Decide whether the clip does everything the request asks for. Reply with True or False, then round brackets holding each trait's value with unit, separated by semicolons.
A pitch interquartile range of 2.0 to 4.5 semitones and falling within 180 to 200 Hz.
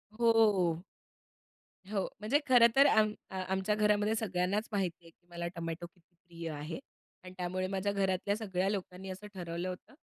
True (3.1 semitones; 190 Hz)